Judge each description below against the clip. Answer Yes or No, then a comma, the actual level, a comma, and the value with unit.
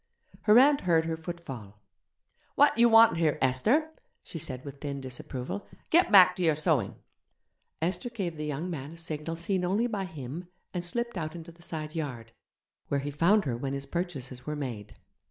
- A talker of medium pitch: Yes, medium, 160 Hz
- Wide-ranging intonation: No, average, 4.8 semitones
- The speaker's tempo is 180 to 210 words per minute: Yes, average, 190 wpm